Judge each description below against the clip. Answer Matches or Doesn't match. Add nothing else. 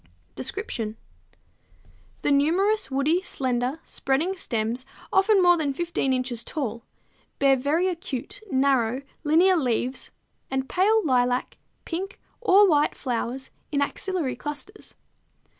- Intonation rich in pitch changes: Matches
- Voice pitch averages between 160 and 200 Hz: Doesn't match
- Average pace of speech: Doesn't match